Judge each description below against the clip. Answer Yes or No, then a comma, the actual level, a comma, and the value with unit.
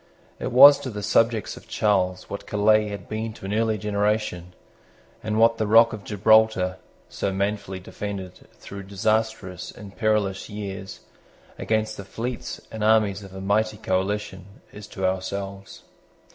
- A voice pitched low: Yes, low, 105 Hz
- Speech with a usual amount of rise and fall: No, narrow, 2.1 semitones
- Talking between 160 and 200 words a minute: No, average, 150 wpm